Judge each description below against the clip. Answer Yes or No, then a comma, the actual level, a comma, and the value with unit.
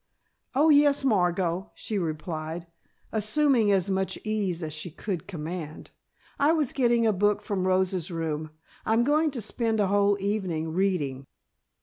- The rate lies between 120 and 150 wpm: Yes, average, 145 wpm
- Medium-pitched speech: No, high, 195 Hz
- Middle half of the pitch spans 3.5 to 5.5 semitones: Yes, average, 4.8 semitones